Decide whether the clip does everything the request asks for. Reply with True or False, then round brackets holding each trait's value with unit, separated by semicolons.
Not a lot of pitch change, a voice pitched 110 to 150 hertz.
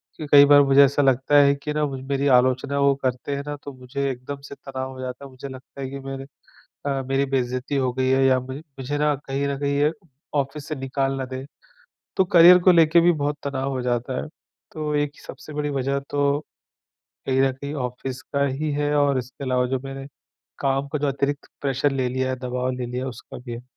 True (1.6 semitones; 135 Hz)